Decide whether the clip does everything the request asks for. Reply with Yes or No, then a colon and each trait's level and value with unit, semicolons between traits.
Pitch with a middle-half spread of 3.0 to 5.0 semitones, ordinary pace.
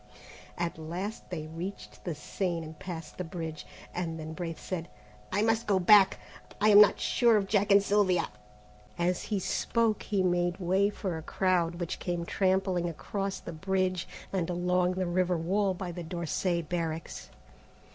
No: narrow, 2.5 semitones; average, 165 wpm